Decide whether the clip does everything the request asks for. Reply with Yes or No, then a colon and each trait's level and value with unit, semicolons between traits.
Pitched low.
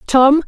No: very high, 280 Hz